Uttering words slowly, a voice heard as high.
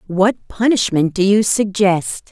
Yes: slow, 130 wpm; high, 195 Hz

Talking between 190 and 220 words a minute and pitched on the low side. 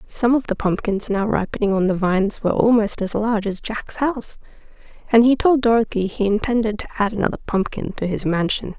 No: average, 200 wpm; high, 215 Hz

